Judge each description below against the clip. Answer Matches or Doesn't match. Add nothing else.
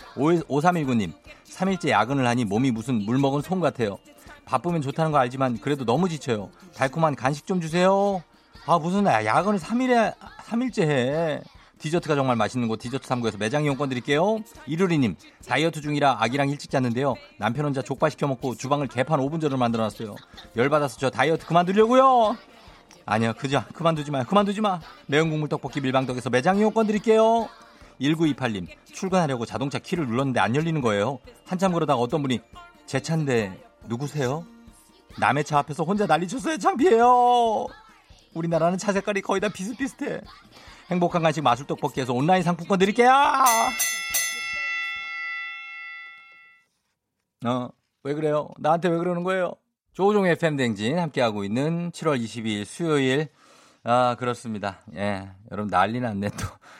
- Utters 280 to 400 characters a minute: Matches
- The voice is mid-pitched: Matches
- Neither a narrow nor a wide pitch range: Doesn't match